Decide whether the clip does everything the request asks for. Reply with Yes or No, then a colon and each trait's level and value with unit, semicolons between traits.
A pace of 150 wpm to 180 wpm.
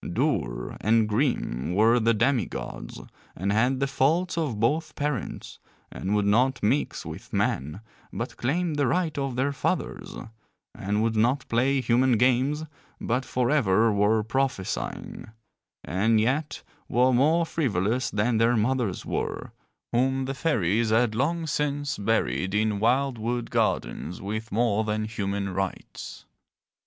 No: average, 140 wpm